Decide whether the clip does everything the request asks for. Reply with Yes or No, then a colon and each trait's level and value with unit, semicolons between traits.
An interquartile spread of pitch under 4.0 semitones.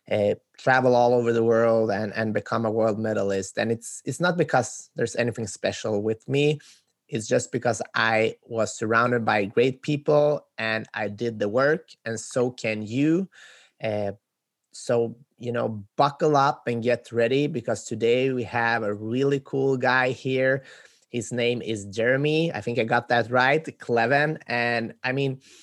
Yes: average, 3.1 semitones